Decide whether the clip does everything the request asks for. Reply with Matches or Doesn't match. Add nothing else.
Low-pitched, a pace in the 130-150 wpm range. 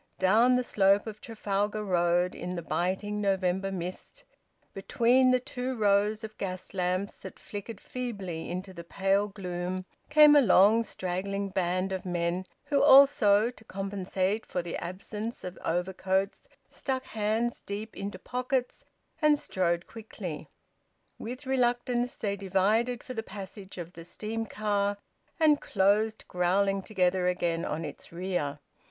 Doesn't match